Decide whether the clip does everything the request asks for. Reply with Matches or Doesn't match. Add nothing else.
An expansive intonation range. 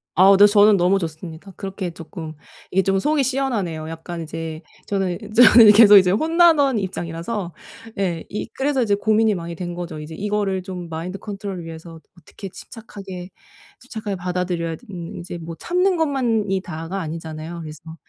Doesn't match